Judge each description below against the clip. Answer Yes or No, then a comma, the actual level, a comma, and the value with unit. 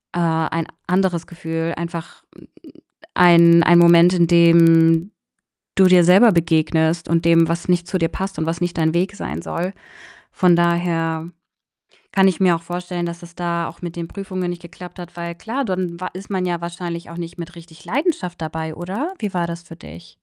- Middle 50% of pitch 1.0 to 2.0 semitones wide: Yes, narrow, 1.3 semitones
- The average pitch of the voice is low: No, medium, 170 Hz